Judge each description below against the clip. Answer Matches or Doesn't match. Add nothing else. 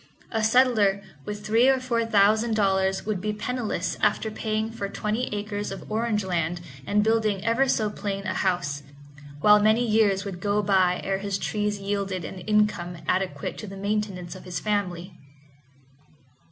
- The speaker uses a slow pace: Doesn't match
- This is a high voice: Matches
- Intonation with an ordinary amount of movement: Doesn't match